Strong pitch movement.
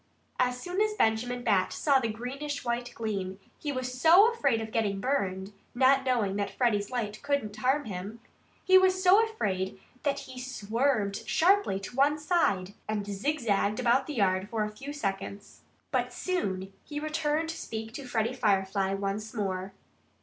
Yes: wide, 5.9 semitones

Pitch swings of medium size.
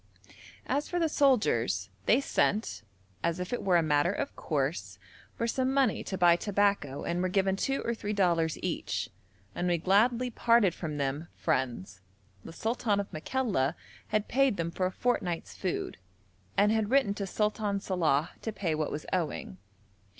No: wide, 5.7 semitones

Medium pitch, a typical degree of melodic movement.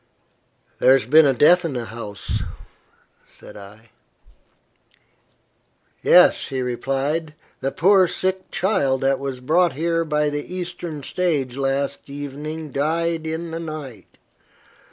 Yes: medium, 145 Hz; average, 3.8 semitones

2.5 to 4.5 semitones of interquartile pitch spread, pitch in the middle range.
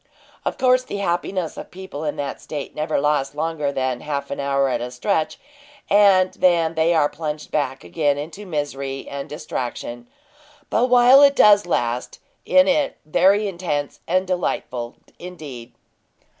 No: average, 5.0 semitones; medium, 155 Hz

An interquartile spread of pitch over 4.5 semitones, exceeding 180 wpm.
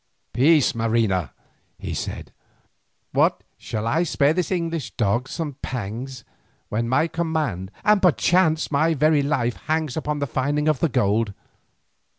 No: wide, 5.6 semitones; average, 140 wpm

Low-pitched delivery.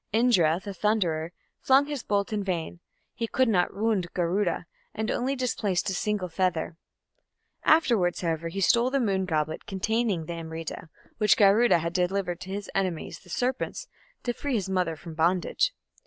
No: high, 190 Hz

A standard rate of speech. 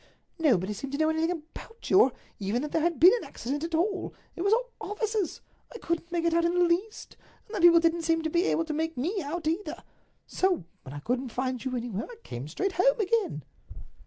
No: fast, 225 wpm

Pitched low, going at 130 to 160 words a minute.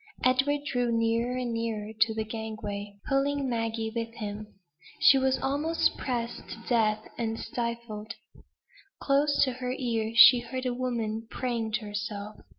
No: high, 230 Hz; average, 150 wpm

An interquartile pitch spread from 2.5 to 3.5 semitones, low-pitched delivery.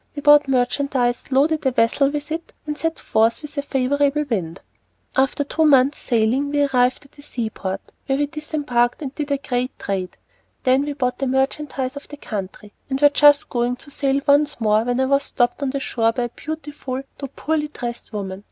No: average, 3.1 semitones; very high, 270 Hz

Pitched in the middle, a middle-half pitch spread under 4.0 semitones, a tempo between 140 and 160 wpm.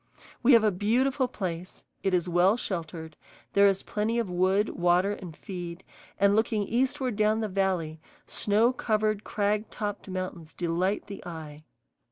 No: high, 200 Hz; average, 3.4 semitones; average, 155 wpm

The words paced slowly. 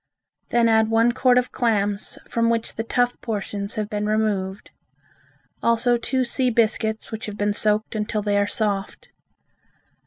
No: average, 155 wpm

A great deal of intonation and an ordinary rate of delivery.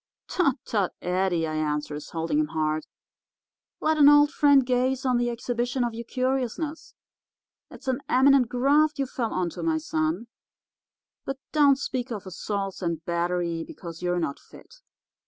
Yes: wide, 7.9 semitones; average, 155 wpm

